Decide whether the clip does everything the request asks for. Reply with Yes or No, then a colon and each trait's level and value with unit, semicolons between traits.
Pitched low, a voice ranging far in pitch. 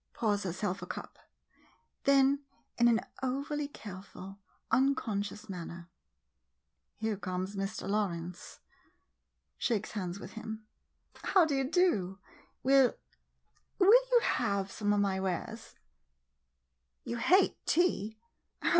No: high, 215 Hz; wide, 5.7 semitones